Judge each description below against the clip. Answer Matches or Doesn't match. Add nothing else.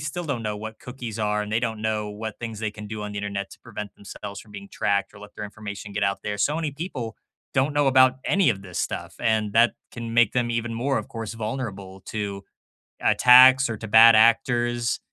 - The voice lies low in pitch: Matches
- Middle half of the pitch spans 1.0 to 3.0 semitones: Matches